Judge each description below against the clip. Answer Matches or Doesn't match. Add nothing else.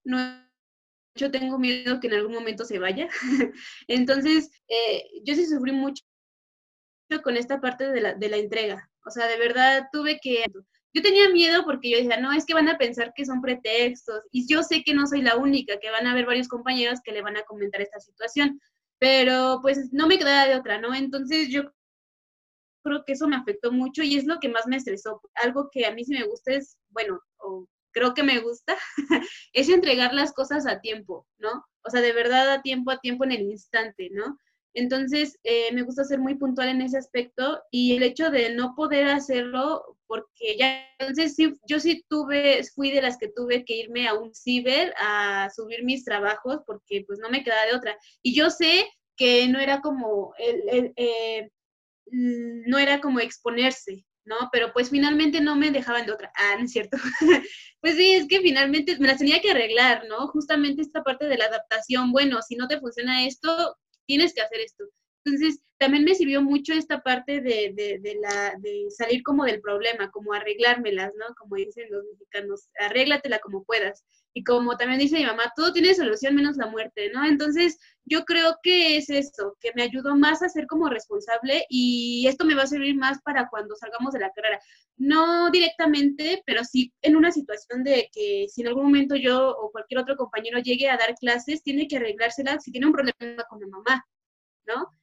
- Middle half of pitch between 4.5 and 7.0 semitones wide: Doesn't match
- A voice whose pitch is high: Matches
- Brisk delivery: Matches